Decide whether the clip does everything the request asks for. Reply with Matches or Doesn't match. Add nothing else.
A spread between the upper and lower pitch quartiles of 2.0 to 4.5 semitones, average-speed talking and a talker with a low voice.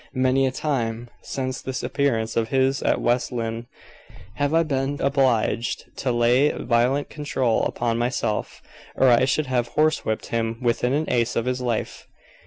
Matches